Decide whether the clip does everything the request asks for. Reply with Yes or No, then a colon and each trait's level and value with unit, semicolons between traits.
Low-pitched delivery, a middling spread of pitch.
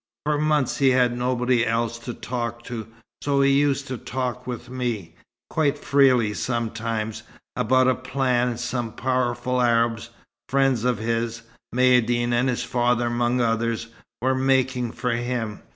No: low, 125 Hz; narrow, 1.7 semitones